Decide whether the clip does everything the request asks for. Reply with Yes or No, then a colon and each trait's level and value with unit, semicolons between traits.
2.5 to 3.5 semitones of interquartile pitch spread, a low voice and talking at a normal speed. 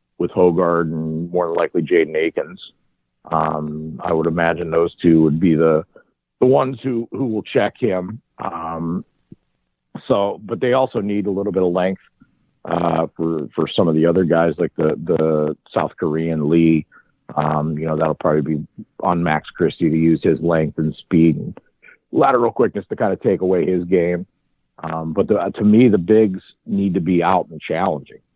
Yes: average, 2.9 semitones; very low, 85 Hz; average, 185 wpm